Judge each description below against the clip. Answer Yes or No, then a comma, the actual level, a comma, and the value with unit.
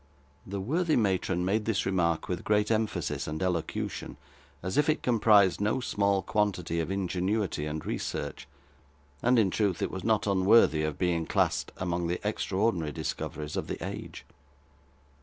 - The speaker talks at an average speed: Yes, average, 155 wpm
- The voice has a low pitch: Yes, very low, 95 Hz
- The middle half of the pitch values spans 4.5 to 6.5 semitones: No, average, 3.7 semitones